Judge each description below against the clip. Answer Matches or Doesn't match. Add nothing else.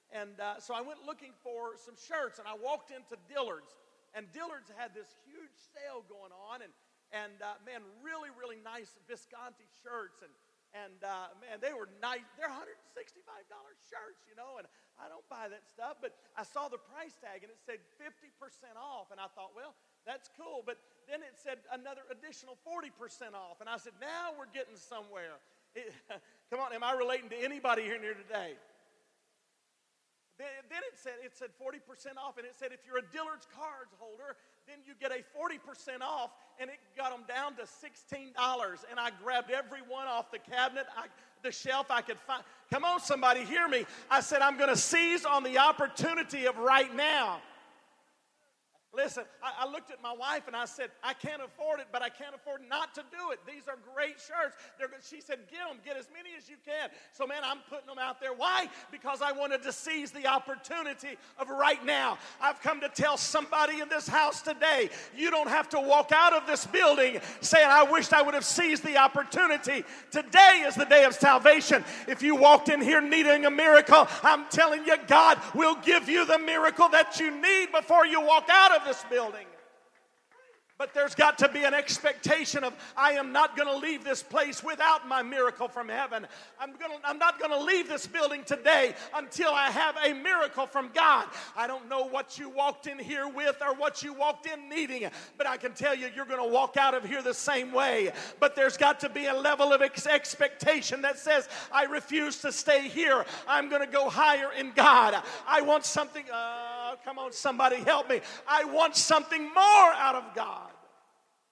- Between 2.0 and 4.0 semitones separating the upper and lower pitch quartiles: Matches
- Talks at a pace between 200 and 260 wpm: Matches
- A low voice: Doesn't match